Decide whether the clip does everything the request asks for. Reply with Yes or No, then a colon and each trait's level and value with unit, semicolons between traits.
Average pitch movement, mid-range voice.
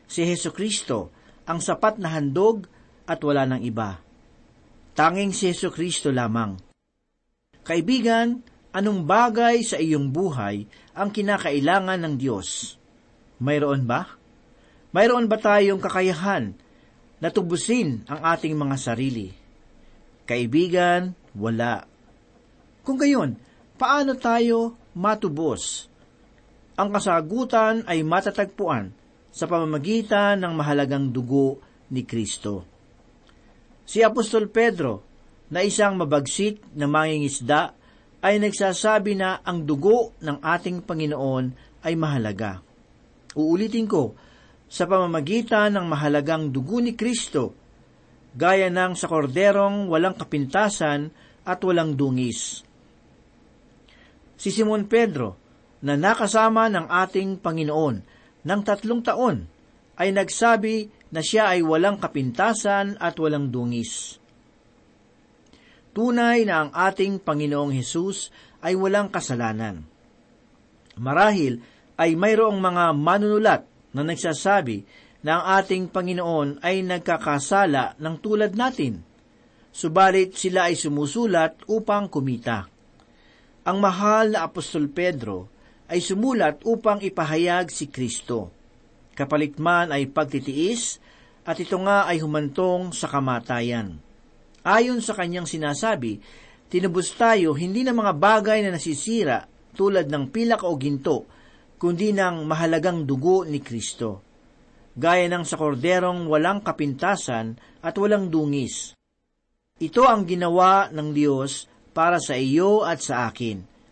No: wide, 5.9 semitones; medium, 175 Hz